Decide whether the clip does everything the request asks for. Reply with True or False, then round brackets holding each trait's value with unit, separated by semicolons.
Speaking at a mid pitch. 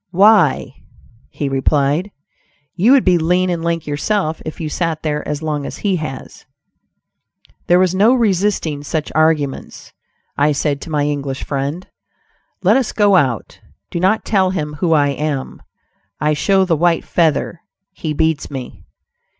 True (160 Hz)